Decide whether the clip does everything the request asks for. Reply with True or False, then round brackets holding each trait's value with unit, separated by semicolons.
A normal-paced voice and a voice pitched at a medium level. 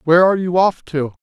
False (245 wpm; 165 Hz)